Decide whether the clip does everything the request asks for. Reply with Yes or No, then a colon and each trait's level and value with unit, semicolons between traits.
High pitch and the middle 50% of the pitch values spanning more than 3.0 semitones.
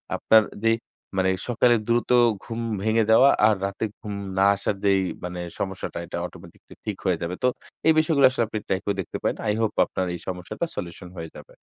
No: low, 105 Hz; average, 3.8 semitones